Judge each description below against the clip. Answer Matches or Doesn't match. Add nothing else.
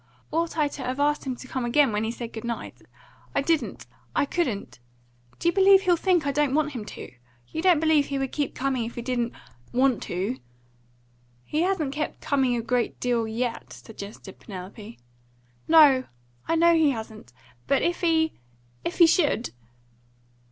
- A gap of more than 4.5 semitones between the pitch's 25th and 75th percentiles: Matches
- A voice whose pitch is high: Matches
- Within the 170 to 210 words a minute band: Matches